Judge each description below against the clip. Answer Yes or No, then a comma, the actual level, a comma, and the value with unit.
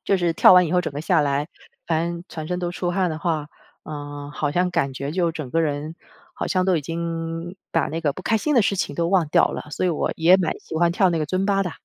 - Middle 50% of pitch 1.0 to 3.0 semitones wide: Yes, average, 2.7 semitones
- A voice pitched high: No, medium, 165 Hz